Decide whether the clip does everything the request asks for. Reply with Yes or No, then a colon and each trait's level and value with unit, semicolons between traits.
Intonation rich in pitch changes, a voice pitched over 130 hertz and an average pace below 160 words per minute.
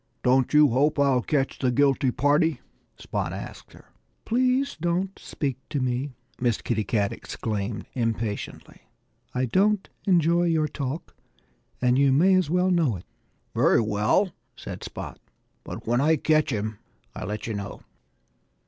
Yes: wide, 5.8 semitones; medium, 140 Hz; average, 150 wpm